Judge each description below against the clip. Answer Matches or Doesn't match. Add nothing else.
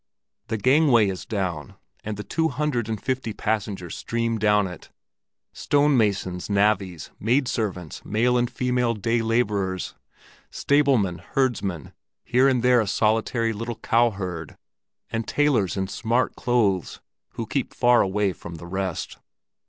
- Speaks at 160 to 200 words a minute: Doesn't match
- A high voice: Doesn't match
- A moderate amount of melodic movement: Matches